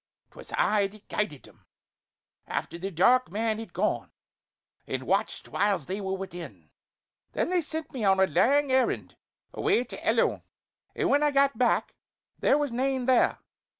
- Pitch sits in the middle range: No, high, 220 Hz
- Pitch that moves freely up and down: Yes, wide, 5.8 semitones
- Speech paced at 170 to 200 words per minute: No, average, 160 wpm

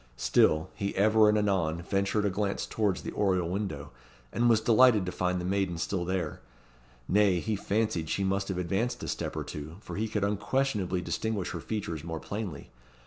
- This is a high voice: No, low, 100 Hz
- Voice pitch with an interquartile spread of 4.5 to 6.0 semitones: No, average, 3.2 semitones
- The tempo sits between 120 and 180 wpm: No, average, 190 wpm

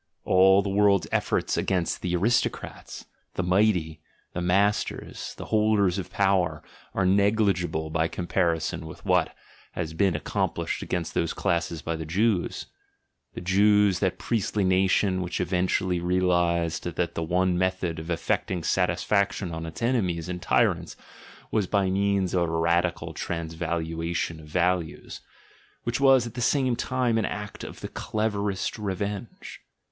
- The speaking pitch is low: Yes, very low, 90 Hz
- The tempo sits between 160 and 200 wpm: No, average, 145 wpm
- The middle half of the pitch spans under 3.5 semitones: Yes, average, 3.1 semitones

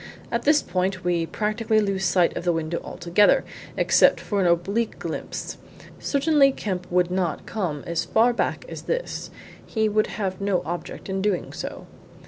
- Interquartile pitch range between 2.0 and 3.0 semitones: No, average, 3.8 semitones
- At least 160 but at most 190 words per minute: Yes, average, 165 wpm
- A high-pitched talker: Yes, high, 195 Hz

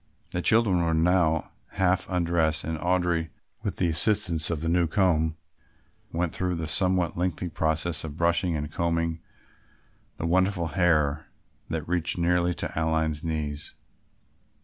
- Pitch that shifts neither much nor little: No, narrow, 1.9 semitones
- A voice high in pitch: No, very low, 85 Hz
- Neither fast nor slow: Yes, average, 145 wpm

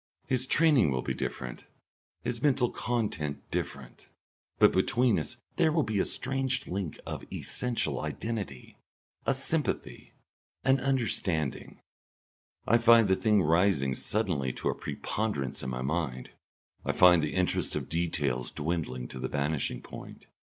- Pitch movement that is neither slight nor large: No, wide, 8.9 semitones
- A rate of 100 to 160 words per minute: Yes, average, 140 wpm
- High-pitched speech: No, very low, 90 Hz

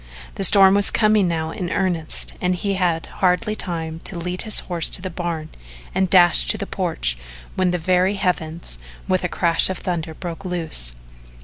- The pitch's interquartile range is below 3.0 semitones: Yes, narrow, 2.4 semitones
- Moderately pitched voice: Yes, medium, 180 Hz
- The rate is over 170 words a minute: Yes, average, 185 wpm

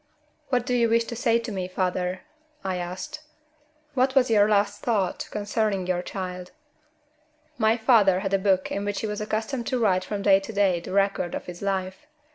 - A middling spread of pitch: Yes, average, 3.3 semitones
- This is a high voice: Yes, high, 200 Hz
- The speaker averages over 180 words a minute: Yes, average, 195 wpm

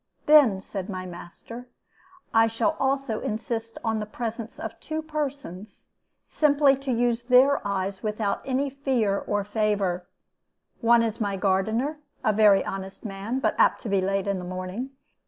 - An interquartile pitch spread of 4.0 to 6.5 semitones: Yes, average, 4.8 semitones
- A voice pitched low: No, high, 220 Hz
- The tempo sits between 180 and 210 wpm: No, average, 155 wpm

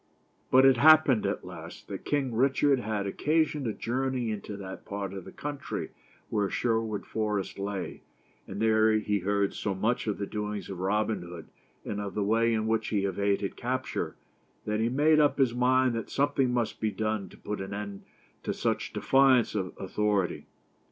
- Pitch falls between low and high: No, low, 110 Hz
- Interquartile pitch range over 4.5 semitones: No, average, 4.0 semitones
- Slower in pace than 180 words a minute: No, average, 185 wpm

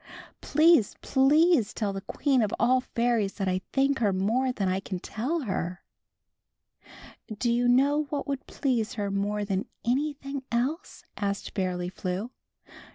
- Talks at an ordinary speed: Yes, average, 165 wpm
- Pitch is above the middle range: Yes, high, 235 Hz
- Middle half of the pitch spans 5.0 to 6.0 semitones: Yes, wide, 5.5 semitones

